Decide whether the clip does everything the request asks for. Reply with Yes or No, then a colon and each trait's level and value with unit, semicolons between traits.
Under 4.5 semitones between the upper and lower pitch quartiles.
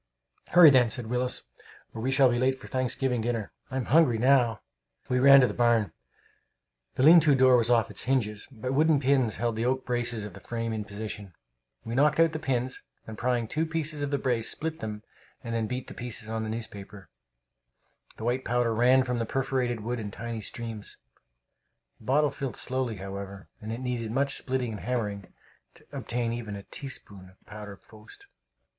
Yes: average, 3.0 semitones